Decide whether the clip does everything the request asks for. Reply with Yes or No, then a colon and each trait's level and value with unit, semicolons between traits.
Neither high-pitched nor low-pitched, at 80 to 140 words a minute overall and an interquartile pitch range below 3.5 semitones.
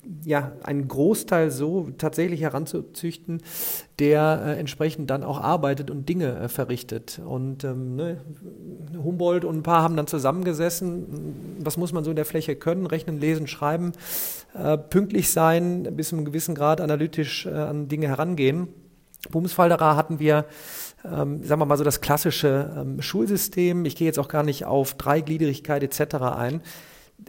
No: medium, 155 Hz; average, 160 wpm; narrow, 2.4 semitones